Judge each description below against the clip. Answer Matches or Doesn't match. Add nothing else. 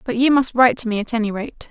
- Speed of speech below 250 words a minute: Doesn't match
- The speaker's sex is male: Doesn't match